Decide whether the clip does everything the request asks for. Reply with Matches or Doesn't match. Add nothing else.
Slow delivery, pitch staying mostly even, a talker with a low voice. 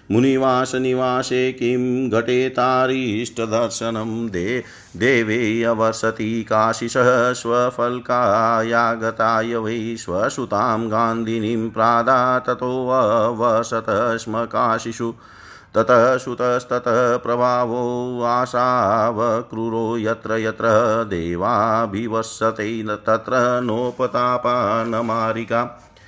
Matches